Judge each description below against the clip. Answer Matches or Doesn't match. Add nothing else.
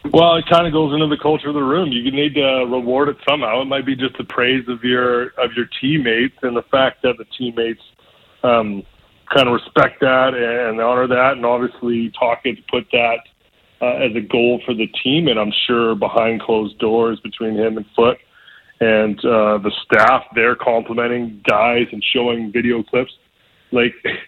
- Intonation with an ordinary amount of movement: Doesn't match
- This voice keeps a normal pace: Matches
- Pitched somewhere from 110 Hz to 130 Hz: Matches